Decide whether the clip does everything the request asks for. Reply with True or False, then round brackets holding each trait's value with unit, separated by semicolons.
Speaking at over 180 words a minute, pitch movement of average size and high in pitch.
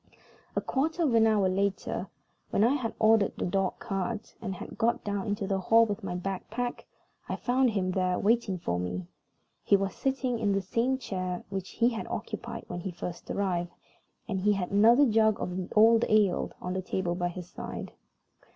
True (195 wpm; 3.7 semitones; 200 Hz)